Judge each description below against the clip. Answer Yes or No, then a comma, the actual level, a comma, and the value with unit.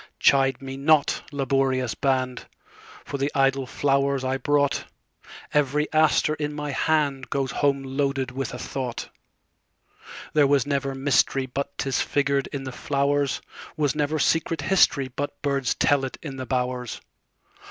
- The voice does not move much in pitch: Yes, narrow, 1.4 semitones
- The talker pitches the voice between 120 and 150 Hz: Yes, medium, 140 Hz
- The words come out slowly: Yes, slow, 120 wpm